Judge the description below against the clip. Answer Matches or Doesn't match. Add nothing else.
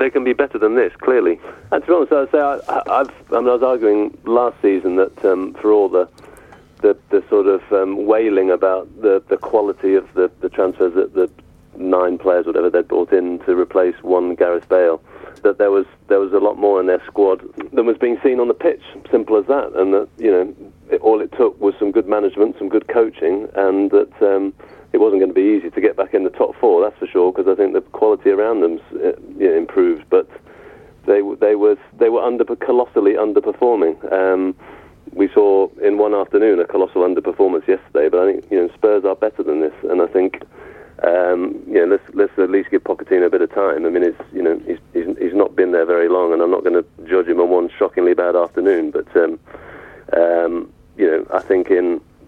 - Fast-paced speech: Matches